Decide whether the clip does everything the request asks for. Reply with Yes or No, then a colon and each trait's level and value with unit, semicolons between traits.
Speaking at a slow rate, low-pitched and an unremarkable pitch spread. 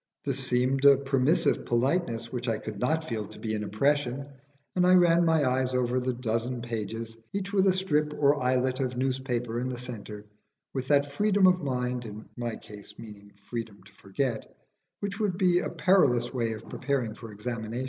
No: average, 190 wpm; low, 125 Hz; average, 4.0 semitones